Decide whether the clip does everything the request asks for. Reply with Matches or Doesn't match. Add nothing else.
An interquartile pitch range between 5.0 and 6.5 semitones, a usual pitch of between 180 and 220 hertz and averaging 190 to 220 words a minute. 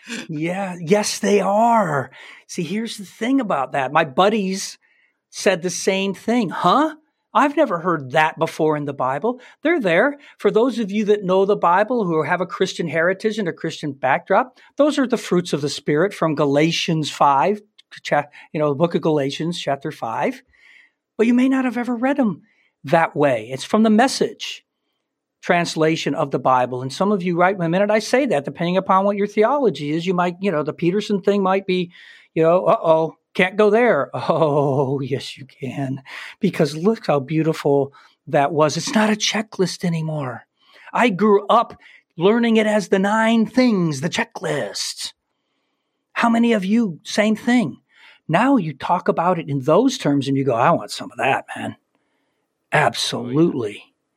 Doesn't match